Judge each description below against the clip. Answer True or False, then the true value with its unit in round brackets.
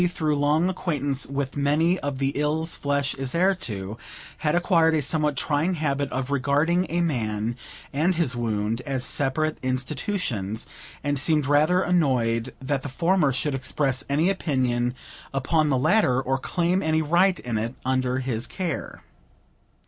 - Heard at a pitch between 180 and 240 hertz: False (145 Hz)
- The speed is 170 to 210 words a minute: False (155 wpm)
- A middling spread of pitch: True (3.9 semitones)